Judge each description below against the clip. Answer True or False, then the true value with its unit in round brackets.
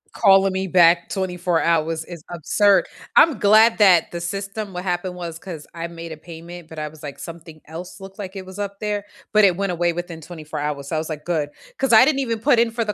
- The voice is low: False (175 Hz)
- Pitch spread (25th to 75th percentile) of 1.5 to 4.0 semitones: True (3.3 semitones)